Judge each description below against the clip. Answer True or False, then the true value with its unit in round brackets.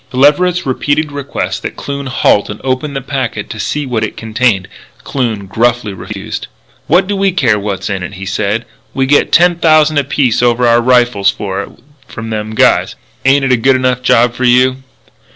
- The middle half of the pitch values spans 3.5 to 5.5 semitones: True (4.3 semitones)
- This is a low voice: True (125 Hz)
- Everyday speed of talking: True (190 wpm)